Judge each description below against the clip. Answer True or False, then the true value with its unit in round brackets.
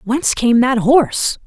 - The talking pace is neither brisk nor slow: True (165 wpm)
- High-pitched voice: True (245 Hz)